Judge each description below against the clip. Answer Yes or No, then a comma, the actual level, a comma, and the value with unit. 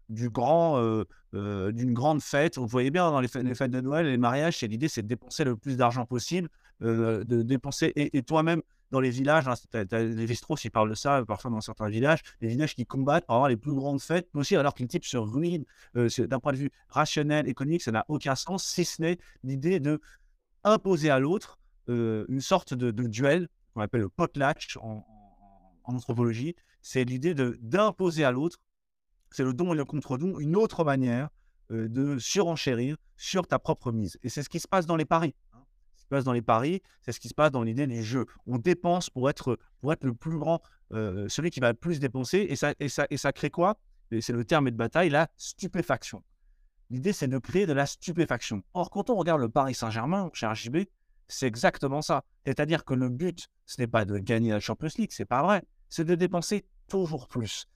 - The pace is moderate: No, fast, 230 wpm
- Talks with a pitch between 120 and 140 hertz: Yes, low, 135 Hz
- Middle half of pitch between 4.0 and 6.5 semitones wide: Yes, wide, 5.4 semitones